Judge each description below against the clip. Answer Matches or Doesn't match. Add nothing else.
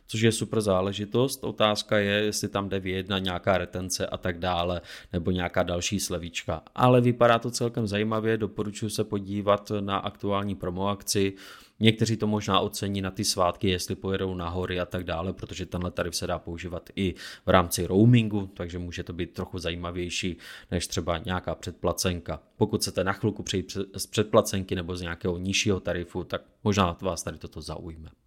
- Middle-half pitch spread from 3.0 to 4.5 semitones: Doesn't match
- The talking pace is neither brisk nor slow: Doesn't match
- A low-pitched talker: Matches